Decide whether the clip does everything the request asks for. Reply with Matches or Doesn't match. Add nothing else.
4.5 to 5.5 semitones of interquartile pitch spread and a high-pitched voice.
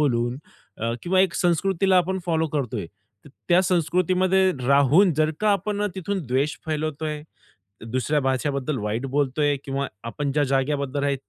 Doesn't match